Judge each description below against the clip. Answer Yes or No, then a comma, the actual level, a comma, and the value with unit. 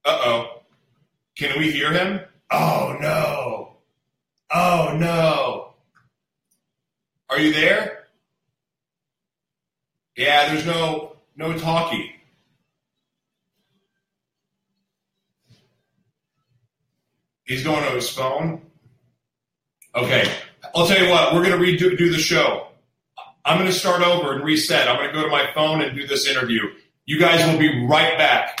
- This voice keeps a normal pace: No, slow, 120 wpm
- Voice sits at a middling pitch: Yes, medium, 155 Hz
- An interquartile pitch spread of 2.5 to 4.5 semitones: Yes, average, 3.2 semitones